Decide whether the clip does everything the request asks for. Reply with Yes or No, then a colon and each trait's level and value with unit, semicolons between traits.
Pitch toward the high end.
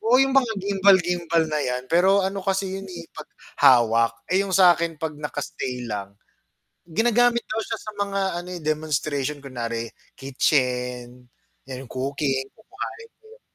No: medium, 155 Hz